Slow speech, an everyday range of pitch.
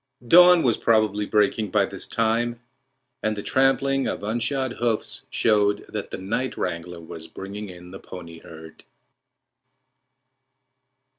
Yes: slow, 130 wpm; average, 4.0 semitones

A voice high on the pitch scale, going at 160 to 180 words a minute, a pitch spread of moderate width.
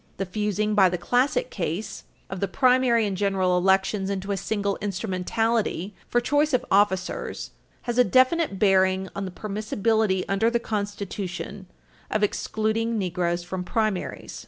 No: high, 200 Hz; average, 145 wpm; average, 3.0 semitones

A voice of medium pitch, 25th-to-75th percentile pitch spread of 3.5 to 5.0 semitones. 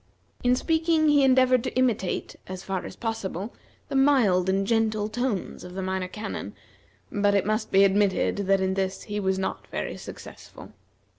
No: high, 205 Hz; average, 4.6 semitones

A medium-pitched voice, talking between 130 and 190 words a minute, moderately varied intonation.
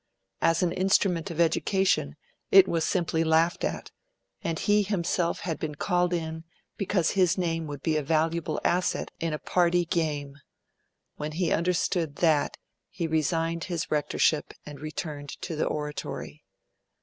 No: medium, 165 Hz; average, 150 wpm; narrow, 2.3 semitones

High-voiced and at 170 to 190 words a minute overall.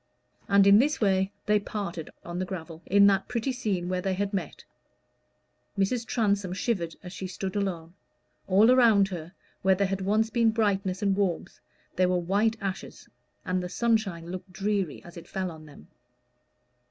Yes: high, 195 Hz; average, 175 wpm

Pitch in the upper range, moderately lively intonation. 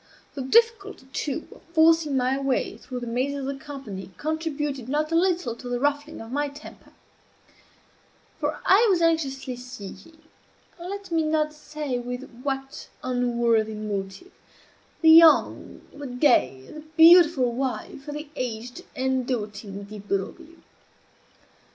Yes: very high, 275 Hz; average, 4.3 semitones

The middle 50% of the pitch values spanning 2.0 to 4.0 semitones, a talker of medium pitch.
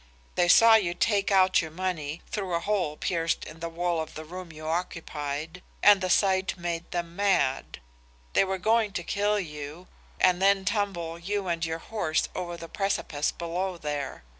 Yes: average, 2.9 semitones; medium, 175 Hz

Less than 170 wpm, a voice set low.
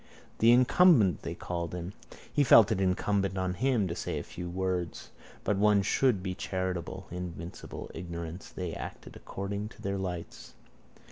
Yes: average, 155 wpm; very low, 95 Hz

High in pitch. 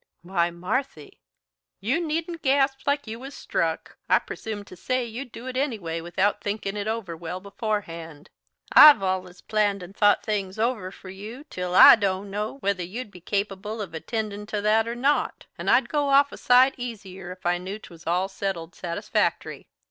Yes: high, 205 Hz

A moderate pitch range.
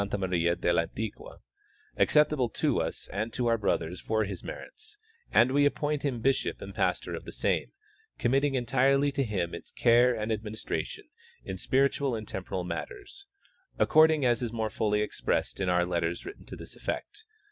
No: wide, 6.1 semitones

